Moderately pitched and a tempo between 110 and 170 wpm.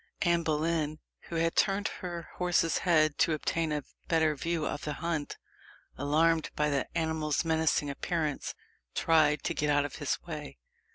Yes: medium, 160 Hz; average, 160 wpm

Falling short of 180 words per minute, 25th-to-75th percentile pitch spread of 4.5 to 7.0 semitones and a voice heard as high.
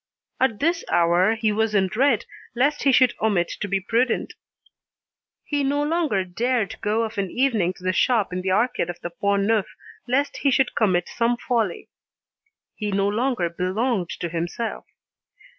Yes: average, 170 wpm; average, 5.0 semitones; high, 220 Hz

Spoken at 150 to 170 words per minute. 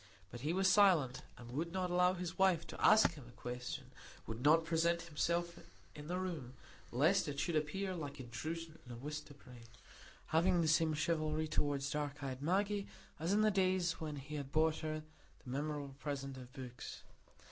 No: average, 190 wpm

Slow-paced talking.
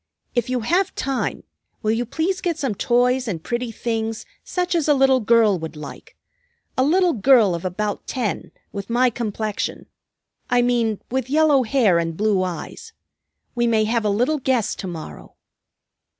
No: average, 165 wpm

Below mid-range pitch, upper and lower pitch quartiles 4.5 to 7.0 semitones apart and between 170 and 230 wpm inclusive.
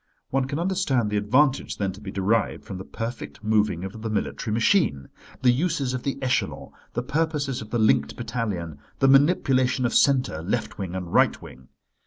Yes: low, 115 Hz; average, 4.8 semitones; average, 185 wpm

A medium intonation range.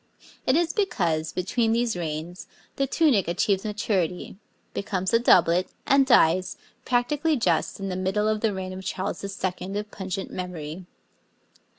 Yes: average, 4.1 semitones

